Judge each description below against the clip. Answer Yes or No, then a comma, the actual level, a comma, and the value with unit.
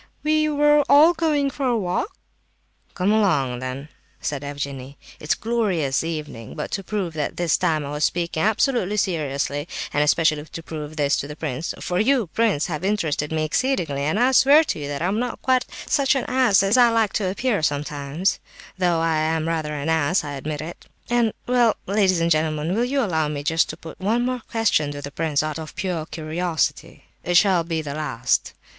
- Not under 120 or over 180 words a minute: No, average, 200 wpm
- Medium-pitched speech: Yes, medium, 165 Hz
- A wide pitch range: Yes, wide, 6.6 semitones